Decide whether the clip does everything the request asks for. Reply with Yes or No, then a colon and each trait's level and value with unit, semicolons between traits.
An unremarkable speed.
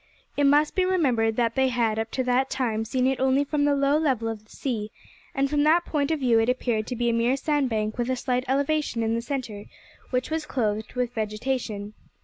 No: fast, 225 wpm